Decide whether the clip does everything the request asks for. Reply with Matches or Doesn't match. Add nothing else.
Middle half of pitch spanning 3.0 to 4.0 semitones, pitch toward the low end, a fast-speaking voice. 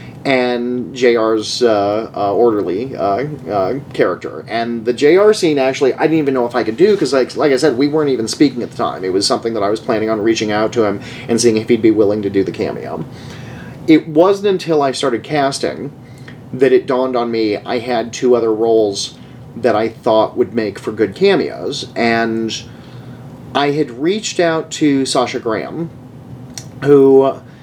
Doesn't match